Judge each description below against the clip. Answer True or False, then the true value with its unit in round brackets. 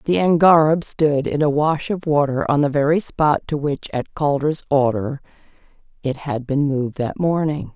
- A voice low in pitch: False (145 Hz)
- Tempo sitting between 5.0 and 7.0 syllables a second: False (4.6 syllables/s)